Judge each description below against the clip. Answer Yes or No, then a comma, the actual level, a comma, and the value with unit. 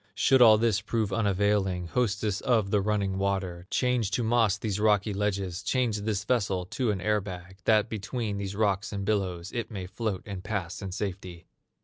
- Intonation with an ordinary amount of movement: No, narrow, 2.3 semitones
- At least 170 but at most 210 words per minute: Yes, average, 180 wpm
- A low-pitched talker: Yes, low, 100 Hz